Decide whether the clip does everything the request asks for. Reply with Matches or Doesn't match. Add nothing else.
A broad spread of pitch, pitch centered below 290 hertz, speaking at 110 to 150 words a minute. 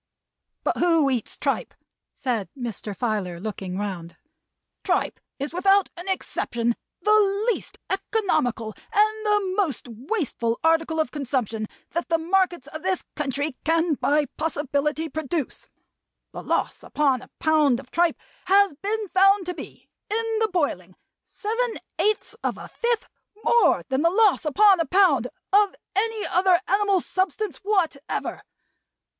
Doesn't match